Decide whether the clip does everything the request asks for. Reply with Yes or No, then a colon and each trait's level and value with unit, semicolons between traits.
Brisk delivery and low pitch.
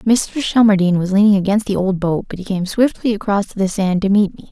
No: fast, 240 wpm; high, 200 Hz